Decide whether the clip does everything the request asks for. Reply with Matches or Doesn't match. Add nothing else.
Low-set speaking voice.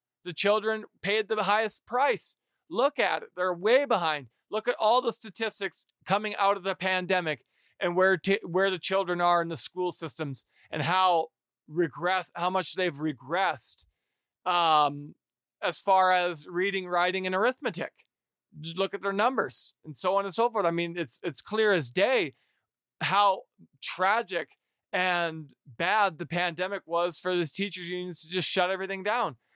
Doesn't match